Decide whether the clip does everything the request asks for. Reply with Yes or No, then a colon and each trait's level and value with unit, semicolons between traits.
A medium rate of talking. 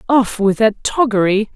Yes: average, 155 wpm